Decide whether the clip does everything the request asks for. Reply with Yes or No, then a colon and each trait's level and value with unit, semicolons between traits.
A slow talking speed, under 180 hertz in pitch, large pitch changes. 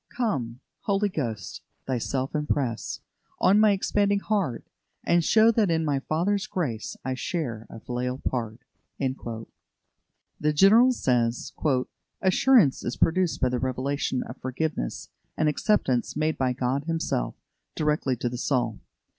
Yes: slow, 130 wpm; medium, 140 Hz; wide, 7.0 semitones